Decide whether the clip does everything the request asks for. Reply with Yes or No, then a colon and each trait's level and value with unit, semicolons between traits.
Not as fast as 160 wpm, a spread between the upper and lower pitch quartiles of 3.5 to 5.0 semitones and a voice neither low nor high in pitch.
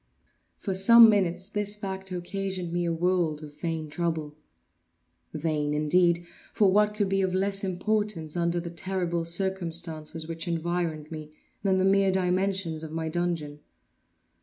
No: average, 145 wpm; average, 2.9 semitones; medium, 175 Hz